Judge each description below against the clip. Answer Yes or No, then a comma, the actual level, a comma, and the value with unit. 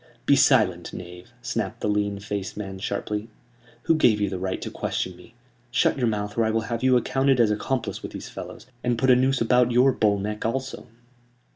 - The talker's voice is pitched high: No, low, 110 Hz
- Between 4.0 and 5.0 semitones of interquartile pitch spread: No, average, 3.6 semitones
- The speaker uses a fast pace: Yes, fast, 210 wpm